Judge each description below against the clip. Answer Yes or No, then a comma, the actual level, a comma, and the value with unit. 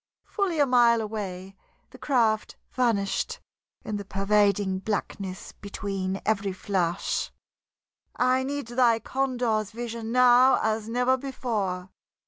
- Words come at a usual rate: No, slow, 110 wpm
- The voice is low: No, high, 220 Hz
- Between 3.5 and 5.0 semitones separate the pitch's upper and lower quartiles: Yes, average, 4.0 semitones